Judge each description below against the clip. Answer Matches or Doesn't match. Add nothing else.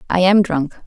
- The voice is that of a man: Doesn't match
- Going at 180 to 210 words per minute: Matches